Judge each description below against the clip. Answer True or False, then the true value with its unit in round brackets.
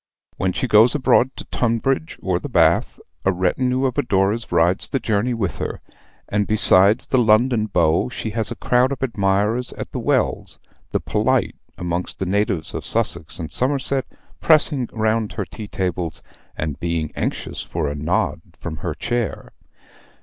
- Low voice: True (105 Hz)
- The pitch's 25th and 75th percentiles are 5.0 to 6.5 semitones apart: True (5.3 semitones)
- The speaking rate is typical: True (165 wpm)